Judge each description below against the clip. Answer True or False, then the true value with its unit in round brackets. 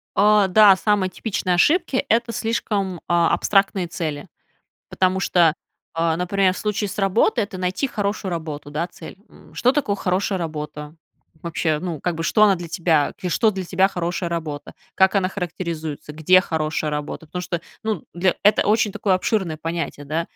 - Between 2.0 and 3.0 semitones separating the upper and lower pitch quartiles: False (3.5 semitones)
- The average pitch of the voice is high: False (180 Hz)